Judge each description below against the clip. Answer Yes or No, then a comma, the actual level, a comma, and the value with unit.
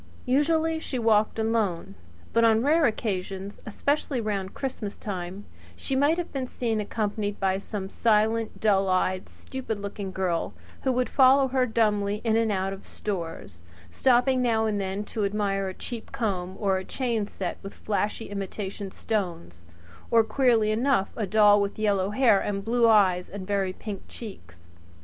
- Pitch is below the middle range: No, high, 210 Hz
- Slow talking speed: No, average, 165 wpm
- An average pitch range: Yes, average, 3.1 semitones